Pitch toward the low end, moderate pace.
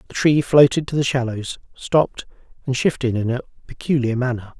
Yes: low, 130 Hz; average, 170 wpm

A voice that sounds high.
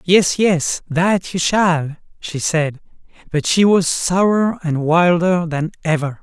No: medium, 170 Hz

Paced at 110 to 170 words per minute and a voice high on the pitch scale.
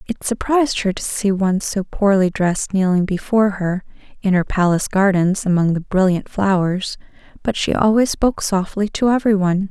Yes: average, 165 wpm; high, 195 Hz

